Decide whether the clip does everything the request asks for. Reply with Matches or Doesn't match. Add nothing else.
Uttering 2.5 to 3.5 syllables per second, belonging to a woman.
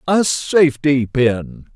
Doesn't match